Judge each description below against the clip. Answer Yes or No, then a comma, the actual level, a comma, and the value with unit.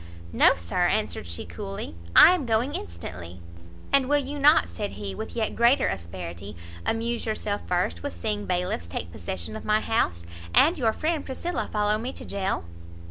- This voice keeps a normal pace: Yes, average, 175 wpm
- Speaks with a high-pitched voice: Yes, high, 205 Hz